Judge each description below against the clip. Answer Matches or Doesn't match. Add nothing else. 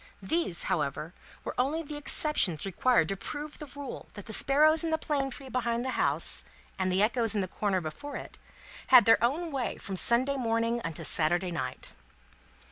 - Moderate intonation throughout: Doesn't match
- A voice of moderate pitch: Doesn't match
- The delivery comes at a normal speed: Matches